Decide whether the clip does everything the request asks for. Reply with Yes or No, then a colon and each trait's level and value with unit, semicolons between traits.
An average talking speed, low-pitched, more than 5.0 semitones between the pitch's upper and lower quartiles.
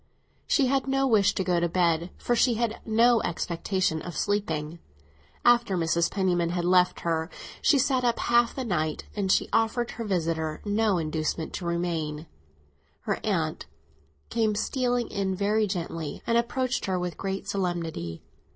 No: average, 160 wpm; high, 190 Hz; wide, 5.4 semitones